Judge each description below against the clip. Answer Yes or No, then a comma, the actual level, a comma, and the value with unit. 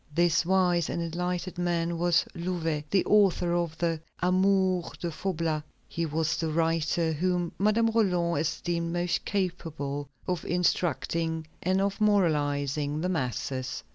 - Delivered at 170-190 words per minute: No, slow, 135 wpm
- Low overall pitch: No, medium, 170 Hz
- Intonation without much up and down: Yes, narrow, 2.0 semitones